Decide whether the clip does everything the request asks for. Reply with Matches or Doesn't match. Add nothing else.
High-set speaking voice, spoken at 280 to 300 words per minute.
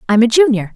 Doesn't match